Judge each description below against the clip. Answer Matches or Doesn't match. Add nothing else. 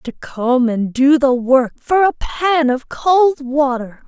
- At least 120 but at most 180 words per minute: Matches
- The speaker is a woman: Matches